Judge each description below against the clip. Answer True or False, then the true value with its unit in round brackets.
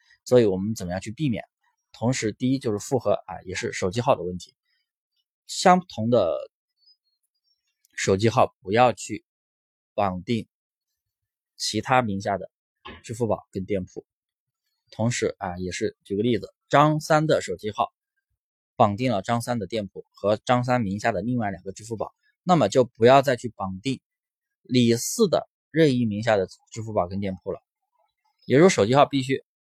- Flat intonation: False (5.5 semitones)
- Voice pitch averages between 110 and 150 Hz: True (115 Hz)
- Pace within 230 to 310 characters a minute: True (235 characters per minute)